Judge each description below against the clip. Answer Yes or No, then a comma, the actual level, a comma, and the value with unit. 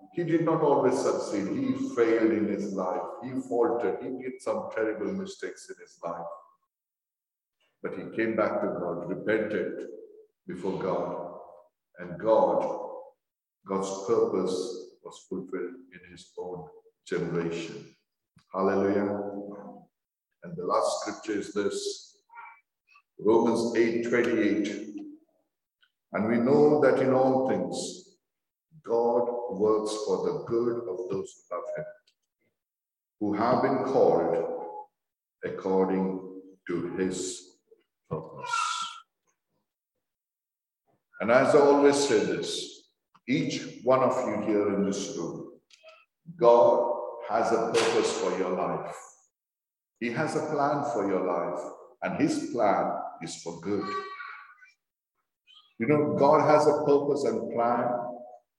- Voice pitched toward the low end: No, medium, 150 Hz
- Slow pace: Yes, slow, 120 wpm